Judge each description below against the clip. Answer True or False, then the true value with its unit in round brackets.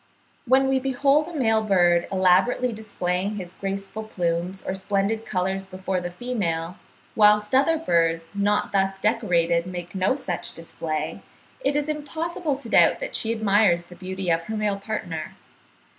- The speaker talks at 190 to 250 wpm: False (155 wpm)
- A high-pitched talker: True (195 Hz)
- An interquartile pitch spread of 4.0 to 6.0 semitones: True (4.4 semitones)